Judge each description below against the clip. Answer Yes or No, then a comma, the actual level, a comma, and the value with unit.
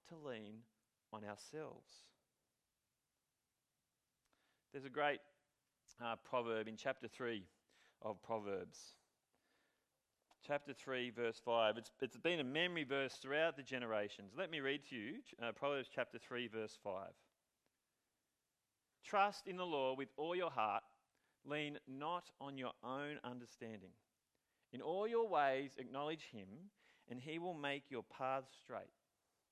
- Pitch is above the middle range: No, low, 135 Hz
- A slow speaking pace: Yes, slow, 130 wpm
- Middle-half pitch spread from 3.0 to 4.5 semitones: Yes, average, 4.0 semitones